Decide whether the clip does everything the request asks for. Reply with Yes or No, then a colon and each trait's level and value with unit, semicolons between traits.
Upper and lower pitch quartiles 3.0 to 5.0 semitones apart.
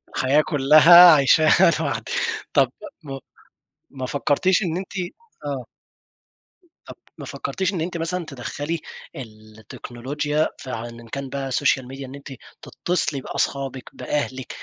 Yes: average, 3.5 semitones